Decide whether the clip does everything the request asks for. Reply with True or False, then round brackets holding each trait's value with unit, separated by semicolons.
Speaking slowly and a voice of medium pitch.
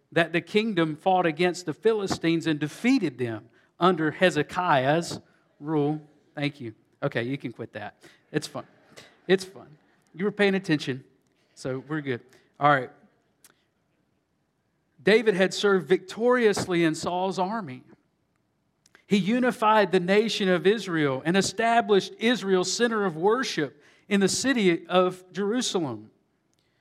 True (130 wpm; 180 Hz)